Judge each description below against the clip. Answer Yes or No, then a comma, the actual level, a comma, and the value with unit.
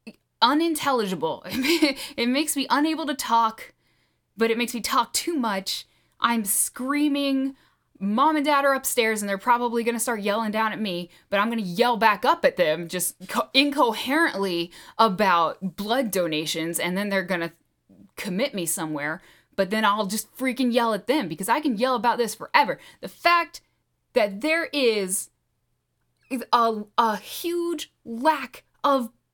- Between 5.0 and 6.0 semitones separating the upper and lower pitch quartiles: Yes, wide, 5.5 semitones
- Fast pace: No, average, 160 wpm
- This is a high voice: Yes, high, 235 Hz